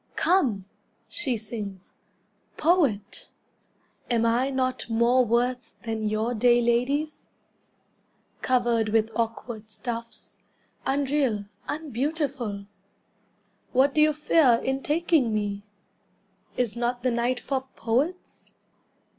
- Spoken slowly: Yes, slow, 100 wpm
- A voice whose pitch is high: Yes, high, 240 Hz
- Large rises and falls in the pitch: No, average, 3.3 semitones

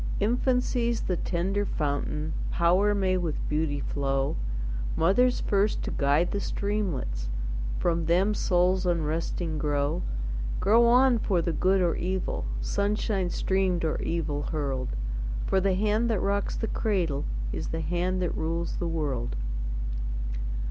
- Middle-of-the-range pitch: Yes, medium, 175 Hz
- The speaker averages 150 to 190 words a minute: No, slow, 135 wpm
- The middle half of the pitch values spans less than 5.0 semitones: Yes, average, 4.4 semitones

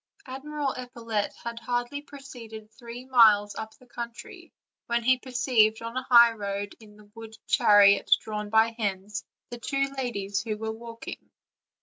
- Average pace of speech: Yes, average, 155 wpm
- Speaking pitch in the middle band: No, high, 230 Hz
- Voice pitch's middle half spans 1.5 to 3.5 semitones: Yes, narrow, 2.6 semitones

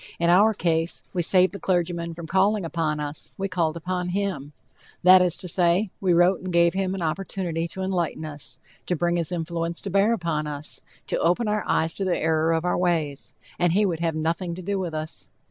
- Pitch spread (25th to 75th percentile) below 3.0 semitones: Yes, narrow, 2.4 semitones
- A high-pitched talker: No, medium, 175 Hz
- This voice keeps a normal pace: No, fast, 215 wpm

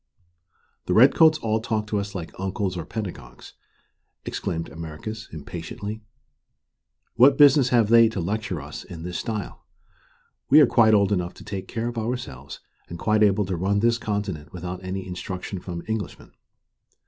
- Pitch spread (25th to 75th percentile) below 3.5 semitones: No, average, 3.8 semitones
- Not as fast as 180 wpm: Yes, average, 160 wpm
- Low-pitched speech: Yes, low, 100 Hz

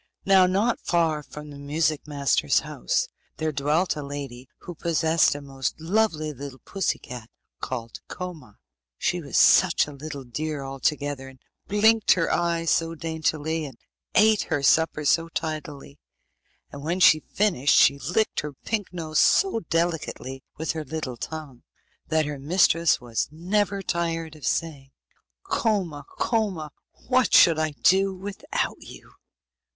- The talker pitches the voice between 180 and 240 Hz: No, medium, 155 Hz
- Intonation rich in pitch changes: No, average, 3.7 semitones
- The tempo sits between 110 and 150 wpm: Yes, average, 145 wpm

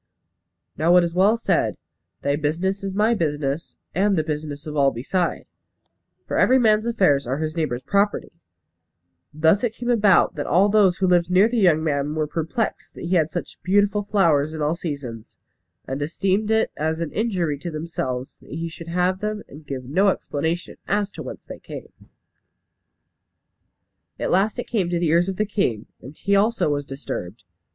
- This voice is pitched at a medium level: Yes, medium, 170 Hz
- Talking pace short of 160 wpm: No, average, 185 wpm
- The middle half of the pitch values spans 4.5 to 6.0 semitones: Yes, average, 5.1 semitones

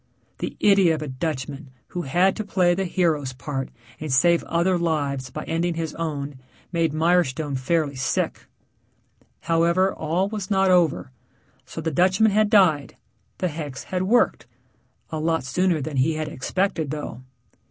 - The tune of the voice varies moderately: Yes, average, 4.0 semitones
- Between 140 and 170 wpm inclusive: Yes, average, 155 wpm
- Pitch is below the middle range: No, medium, 165 Hz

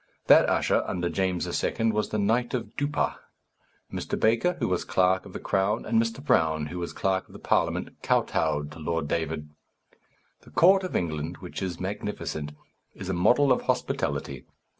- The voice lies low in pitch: Yes, very low, 95 Hz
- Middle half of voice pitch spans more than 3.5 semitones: Yes, wide, 5.6 semitones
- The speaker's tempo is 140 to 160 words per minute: No, average, 175 wpm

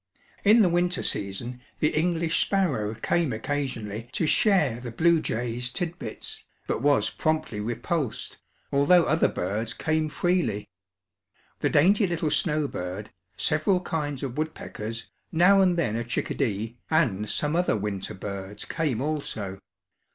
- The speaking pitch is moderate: Yes, medium, 145 Hz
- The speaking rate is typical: No, slow, 130 wpm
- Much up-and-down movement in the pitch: Yes, wide, 7.1 semitones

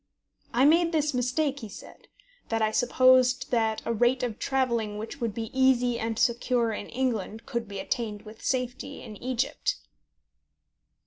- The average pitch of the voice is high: Yes, high, 240 Hz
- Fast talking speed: No, average, 155 wpm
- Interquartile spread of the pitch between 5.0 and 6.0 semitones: No, average, 2.7 semitones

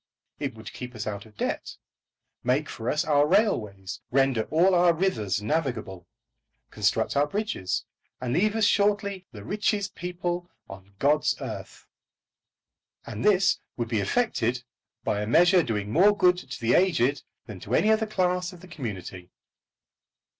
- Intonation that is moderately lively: No, wide, 8.8 semitones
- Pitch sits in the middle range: Yes, medium, 145 Hz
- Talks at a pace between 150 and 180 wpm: Yes, average, 155 wpm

